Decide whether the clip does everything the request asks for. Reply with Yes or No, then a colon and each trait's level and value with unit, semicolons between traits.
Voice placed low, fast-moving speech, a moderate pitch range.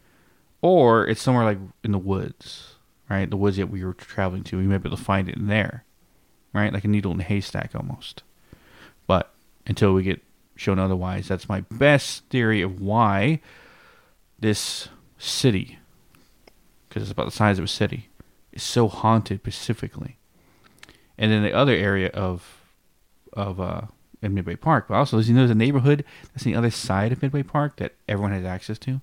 No: low, 105 Hz; average, 185 wpm; average, 3.6 semitones